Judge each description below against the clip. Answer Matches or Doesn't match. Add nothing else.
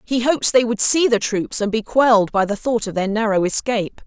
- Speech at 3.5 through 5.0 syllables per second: Doesn't match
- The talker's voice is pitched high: Matches